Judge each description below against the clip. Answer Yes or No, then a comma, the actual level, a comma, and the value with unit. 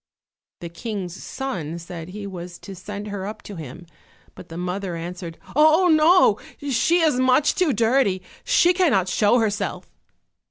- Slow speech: No, average, 155 wpm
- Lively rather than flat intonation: Yes, wide, 7.1 semitones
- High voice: Yes, high, 205 Hz